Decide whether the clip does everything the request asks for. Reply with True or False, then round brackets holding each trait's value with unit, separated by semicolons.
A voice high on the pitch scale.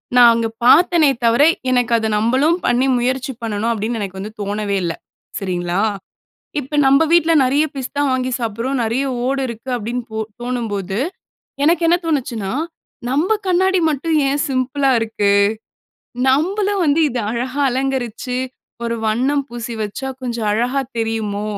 True (250 Hz)